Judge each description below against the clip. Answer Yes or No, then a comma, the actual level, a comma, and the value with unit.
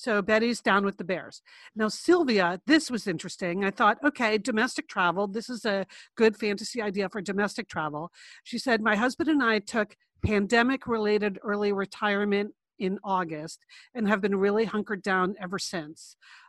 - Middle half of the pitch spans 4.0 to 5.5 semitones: No, average, 2.9 semitones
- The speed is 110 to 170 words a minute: Yes, average, 165 wpm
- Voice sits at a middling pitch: No, high, 210 Hz